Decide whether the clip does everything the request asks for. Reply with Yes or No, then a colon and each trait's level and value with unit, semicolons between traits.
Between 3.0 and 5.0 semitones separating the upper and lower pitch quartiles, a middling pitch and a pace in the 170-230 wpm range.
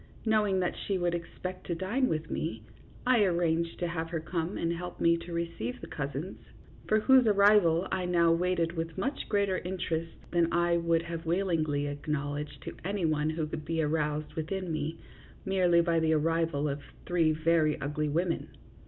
No: narrow, 2.6 semitones; medium, 170 Hz; average, 175 wpm